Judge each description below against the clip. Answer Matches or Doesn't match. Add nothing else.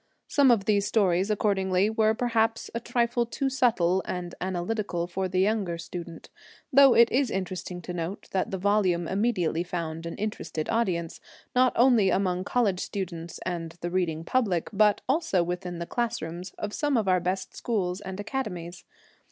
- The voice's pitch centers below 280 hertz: Matches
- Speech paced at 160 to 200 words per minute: Matches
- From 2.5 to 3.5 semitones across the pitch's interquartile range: Doesn't match